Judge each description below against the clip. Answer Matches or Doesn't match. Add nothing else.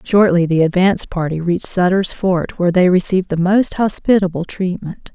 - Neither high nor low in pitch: Matches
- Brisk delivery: Doesn't match